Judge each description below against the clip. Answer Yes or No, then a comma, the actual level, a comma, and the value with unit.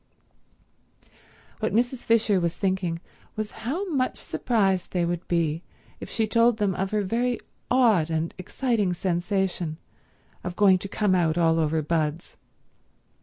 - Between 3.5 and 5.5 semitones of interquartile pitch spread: Yes, average, 4.7 semitones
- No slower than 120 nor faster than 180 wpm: Yes, average, 140 wpm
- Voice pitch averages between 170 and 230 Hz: Yes, high, 190 Hz